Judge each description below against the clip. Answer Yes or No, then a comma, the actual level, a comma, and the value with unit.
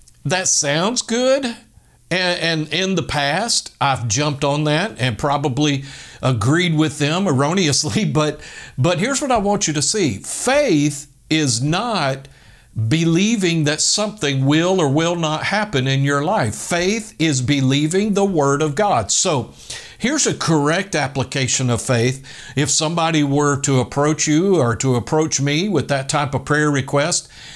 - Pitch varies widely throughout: No, average, 4.0 semitones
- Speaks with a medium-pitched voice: Yes, medium, 150 Hz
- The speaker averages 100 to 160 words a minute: Yes, average, 155 wpm